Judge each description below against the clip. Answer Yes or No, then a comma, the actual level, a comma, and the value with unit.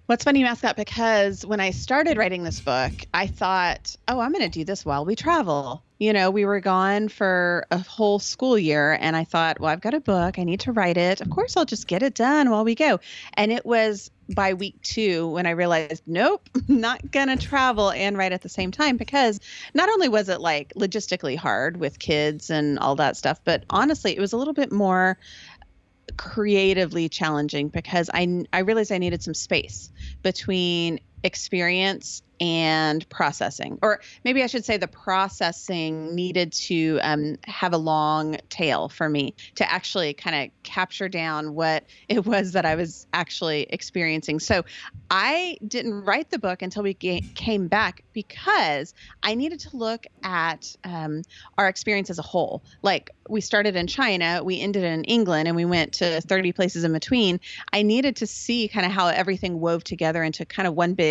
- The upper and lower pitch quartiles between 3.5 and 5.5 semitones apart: Yes, average, 4.7 semitones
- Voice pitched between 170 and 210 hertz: Yes, high, 190 Hz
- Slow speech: No, average, 195 wpm